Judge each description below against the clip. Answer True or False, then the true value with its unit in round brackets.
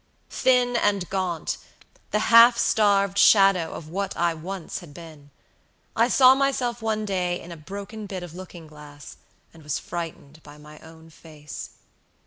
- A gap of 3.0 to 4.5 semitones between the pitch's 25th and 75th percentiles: False (4.9 semitones)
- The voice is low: False (180 Hz)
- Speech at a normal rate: True (155 wpm)